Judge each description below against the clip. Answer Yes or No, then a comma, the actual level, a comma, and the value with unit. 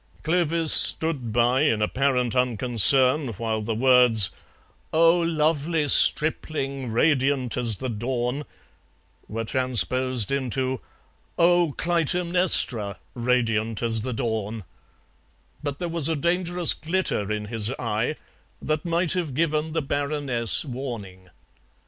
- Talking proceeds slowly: Yes, slow, 110 wpm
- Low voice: Yes, low, 130 Hz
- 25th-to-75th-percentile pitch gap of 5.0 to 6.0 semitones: Yes, average, 5.3 semitones